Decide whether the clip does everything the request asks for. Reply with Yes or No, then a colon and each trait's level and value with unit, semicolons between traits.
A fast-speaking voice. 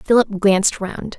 No: average, 150 wpm